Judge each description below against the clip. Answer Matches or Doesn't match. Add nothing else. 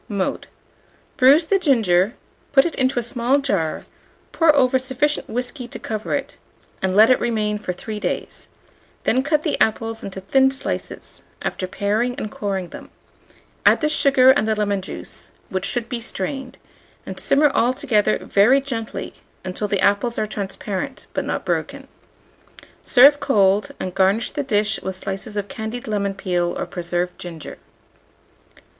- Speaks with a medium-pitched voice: Doesn't match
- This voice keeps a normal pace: Matches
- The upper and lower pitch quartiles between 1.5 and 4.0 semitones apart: Doesn't match